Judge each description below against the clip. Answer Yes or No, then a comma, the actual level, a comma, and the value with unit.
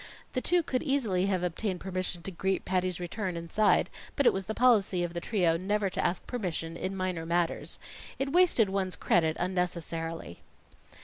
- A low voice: No, medium, 185 Hz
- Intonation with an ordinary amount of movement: Yes, average, 3.4 semitones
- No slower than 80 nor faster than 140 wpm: No, average, 175 wpm